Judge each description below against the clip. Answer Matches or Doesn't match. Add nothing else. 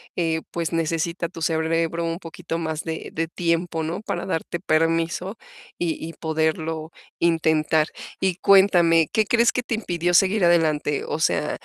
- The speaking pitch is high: Doesn't match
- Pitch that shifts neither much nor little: Doesn't match